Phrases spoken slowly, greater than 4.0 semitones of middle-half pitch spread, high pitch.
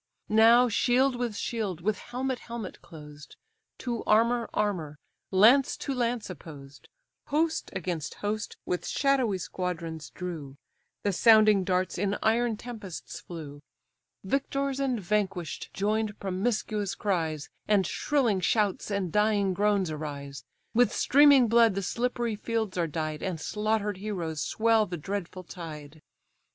Yes: slow, 130 wpm; average, 4.8 semitones; high, 205 Hz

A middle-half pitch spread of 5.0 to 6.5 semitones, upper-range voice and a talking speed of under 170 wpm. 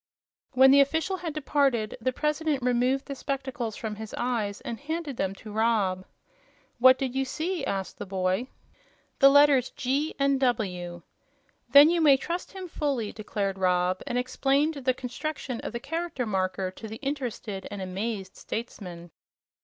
Yes: wide, 5.5 semitones; very high, 250 Hz; average, 160 wpm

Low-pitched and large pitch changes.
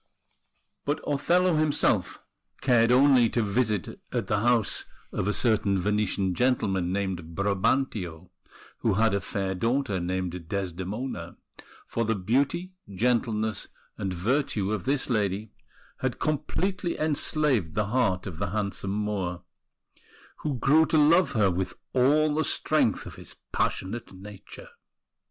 Yes: low, 110 Hz; wide, 5.8 semitones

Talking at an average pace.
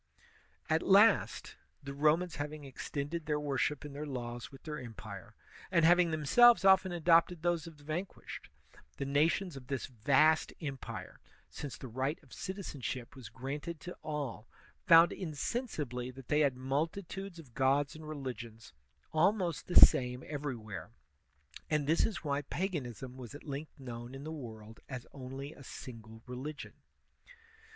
Yes: average, 150 wpm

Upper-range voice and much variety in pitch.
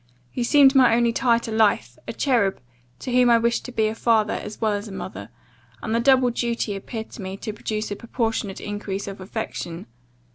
No: high, 225 Hz; narrow, 2.6 semitones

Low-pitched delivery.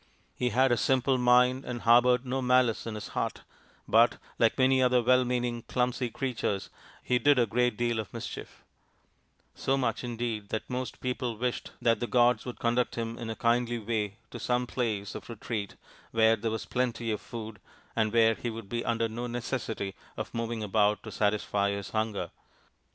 Yes: low, 120 Hz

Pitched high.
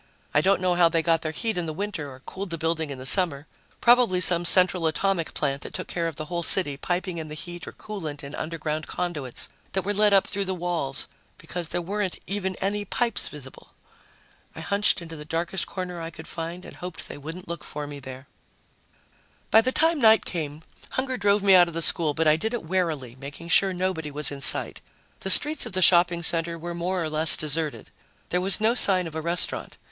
No: medium, 170 Hz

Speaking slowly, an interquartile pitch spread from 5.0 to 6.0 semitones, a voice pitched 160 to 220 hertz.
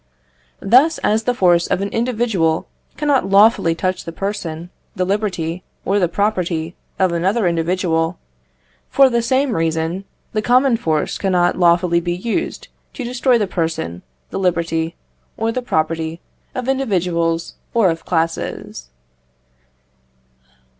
Yes: slow, 130 wpm; average, 5.3 semitones; medium, 185 Hz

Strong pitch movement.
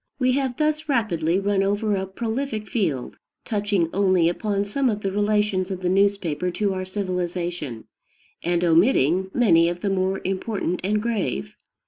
No: average, 3.1 semitones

